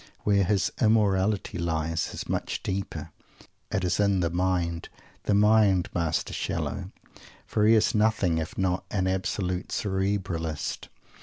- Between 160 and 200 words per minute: No, slow, 135 wpm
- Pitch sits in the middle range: No, very low, 95 Hz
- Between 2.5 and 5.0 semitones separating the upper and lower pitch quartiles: Yes, average, 2.8 semitones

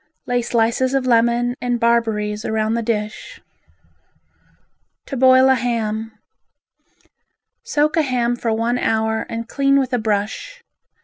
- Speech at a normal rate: No, slow, 130 wpm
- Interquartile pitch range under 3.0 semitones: Yes, narrow, 2.5 semitones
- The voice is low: No, high, 235 Hz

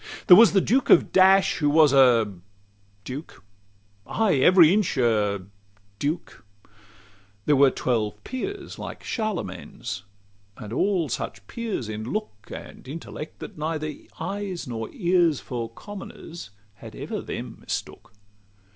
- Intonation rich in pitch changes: Yes, wide, 8.4 semitones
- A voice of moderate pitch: Yes, medium, 155 Hz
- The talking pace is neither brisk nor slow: No, slow, 130 wpm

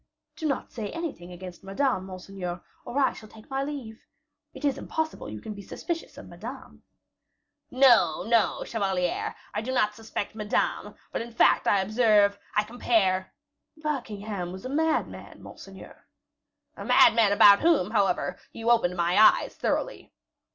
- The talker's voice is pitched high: Yes, high, 215 Hz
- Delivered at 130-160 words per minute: Yes, average, 155 wpm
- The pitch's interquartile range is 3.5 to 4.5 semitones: No, average, 5.2 semitones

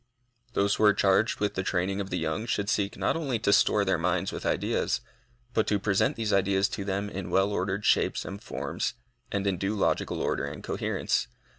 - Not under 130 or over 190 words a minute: No, fast, 205 wpm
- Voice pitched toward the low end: Yes, low, 100 Hz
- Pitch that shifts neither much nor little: No, narrow, 1.4 semitones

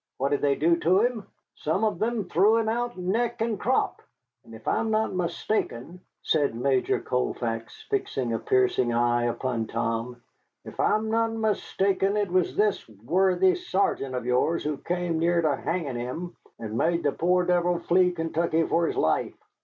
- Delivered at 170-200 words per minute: Yes, average, 175 wpm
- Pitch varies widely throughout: Yes, wide, 7.8 semitones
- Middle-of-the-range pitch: Yes, medium, 170 Hz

